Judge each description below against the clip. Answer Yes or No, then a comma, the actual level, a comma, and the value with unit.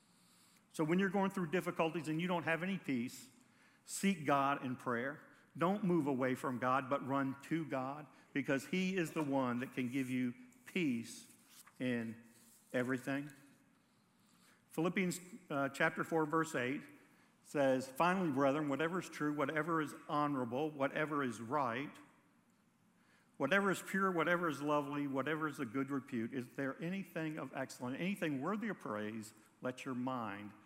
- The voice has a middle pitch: Yes, medium, 150 Hz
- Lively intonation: No, average, 4.7 semitones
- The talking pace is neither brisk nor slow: Yes, average, 155 wpm